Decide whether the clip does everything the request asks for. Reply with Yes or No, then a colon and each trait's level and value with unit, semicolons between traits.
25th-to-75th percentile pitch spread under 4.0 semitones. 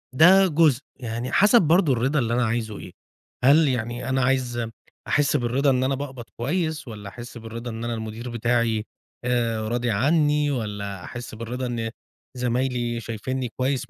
Yes: average, 2.8 semitones